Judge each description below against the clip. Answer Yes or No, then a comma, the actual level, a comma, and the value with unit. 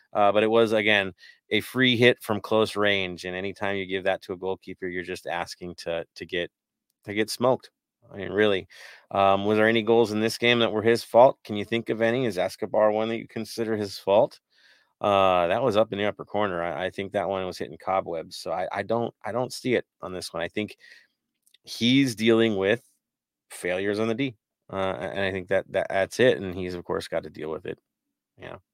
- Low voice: Yes, low, 105 Hz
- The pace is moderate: No, fast, 230 wpm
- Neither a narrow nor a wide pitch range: Yes, average, 3.0 semitones